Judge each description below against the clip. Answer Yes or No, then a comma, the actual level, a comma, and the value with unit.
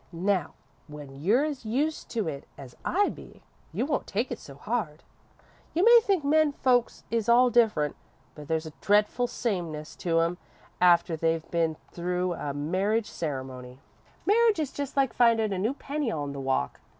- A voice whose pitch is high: Yes, high, 195 Hz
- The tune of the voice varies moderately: No, wide, 8.1 semitones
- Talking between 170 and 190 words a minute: Yes, average, 175 wpm